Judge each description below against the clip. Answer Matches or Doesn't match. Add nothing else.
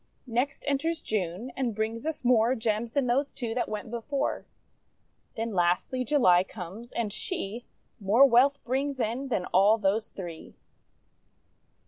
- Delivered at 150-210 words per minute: Doesn't match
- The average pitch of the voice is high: Matches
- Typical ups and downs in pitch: Matches